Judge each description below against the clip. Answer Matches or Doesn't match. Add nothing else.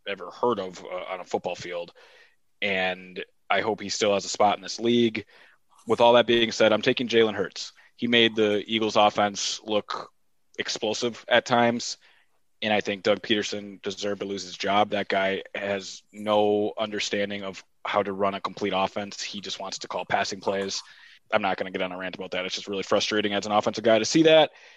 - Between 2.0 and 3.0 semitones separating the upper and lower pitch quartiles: Matches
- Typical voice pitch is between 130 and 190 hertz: Doesn't match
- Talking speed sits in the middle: Doesn't match